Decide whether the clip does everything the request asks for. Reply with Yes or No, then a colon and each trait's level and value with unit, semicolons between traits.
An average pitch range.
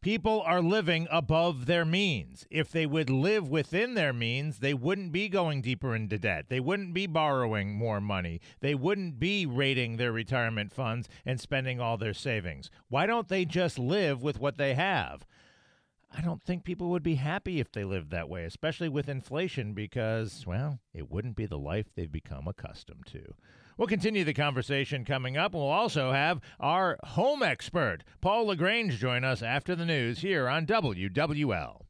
No: wide, 7.0 semitones